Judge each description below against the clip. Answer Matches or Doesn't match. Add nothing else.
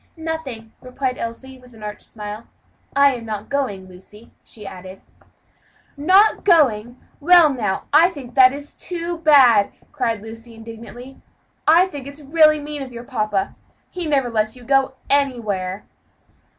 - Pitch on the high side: Matches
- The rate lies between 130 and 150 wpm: Matches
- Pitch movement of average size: Matches